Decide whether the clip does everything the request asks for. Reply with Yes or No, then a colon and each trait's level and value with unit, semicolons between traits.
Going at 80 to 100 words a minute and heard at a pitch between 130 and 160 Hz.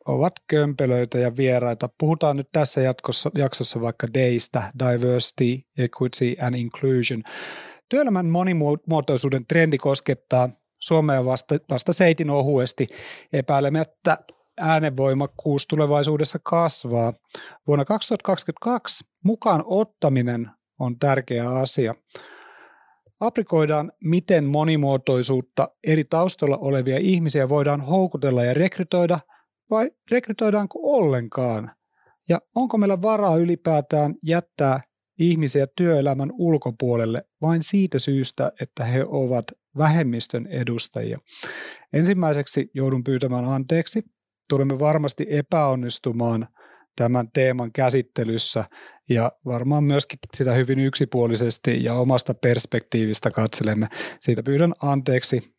Yes: slow, 95 wpm; medium, 140 Hz